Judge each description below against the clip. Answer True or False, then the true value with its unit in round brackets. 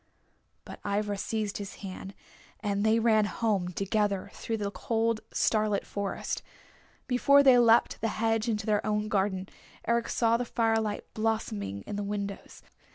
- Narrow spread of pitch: True (2.0 semitones)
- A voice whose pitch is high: True (215 Hz)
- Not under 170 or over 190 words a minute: False (150 wpm)